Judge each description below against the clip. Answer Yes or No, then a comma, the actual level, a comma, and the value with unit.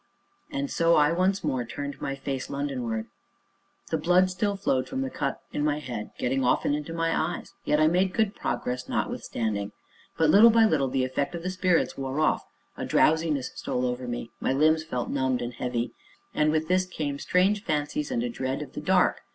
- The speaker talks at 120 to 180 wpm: No, average, 200 wpm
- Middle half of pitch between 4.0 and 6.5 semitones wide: Yes, wide, 5.6 semitones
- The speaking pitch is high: No, medium, 150 Hz